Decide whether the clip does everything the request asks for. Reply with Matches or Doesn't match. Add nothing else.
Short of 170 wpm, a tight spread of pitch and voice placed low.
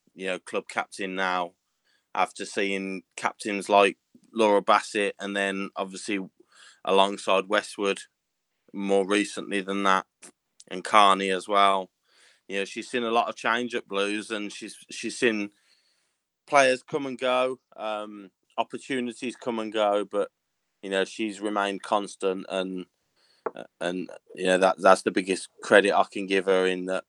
Matches